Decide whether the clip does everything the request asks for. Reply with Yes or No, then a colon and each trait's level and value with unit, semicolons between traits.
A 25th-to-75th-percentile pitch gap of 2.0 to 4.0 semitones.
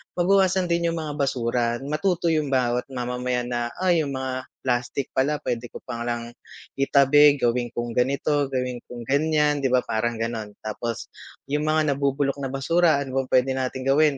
Yes: average, 3.4 semitones